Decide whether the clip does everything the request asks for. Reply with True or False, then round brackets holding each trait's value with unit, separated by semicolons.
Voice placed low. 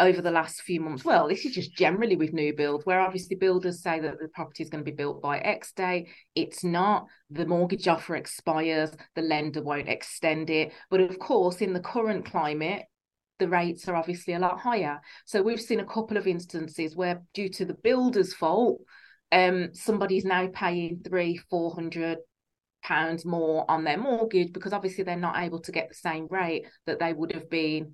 False (175 Hz)